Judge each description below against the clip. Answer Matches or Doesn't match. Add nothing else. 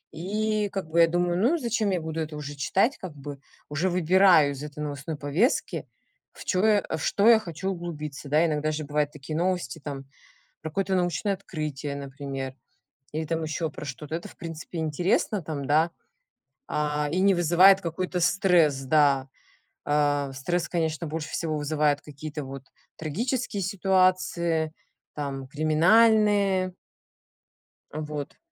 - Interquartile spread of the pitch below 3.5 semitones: Doesn't match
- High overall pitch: Doesn't match